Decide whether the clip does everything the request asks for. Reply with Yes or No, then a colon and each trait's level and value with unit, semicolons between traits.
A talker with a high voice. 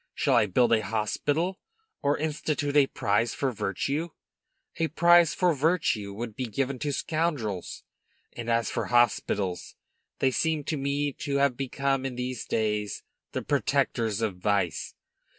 No: low, 130 Hz